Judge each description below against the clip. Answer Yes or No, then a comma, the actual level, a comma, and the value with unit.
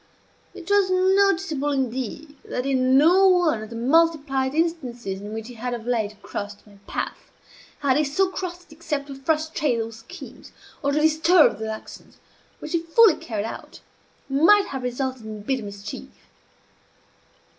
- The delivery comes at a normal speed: Yes, average, 160 wpm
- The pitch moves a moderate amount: No, wide, 6.0 semitones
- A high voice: Yes, very high, 275 Hz